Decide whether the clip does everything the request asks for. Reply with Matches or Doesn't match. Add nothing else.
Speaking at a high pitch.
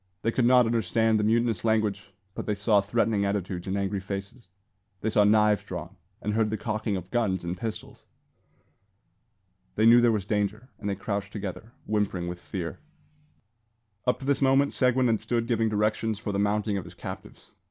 Doesn't match